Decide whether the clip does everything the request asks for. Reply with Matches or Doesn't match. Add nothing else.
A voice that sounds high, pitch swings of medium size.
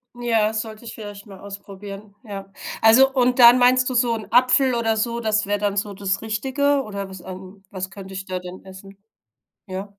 Matches